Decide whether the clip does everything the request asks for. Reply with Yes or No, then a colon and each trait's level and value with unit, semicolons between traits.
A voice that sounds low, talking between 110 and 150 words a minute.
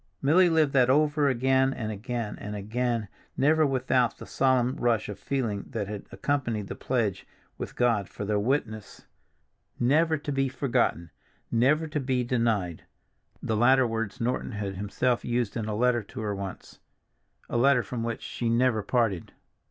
No: low, 120 Hz; average, 160 wpm